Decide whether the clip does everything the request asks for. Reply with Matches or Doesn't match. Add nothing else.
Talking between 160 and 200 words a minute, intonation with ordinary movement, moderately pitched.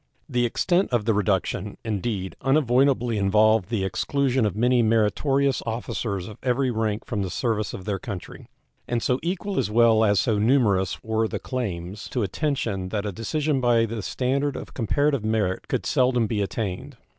Doesn't match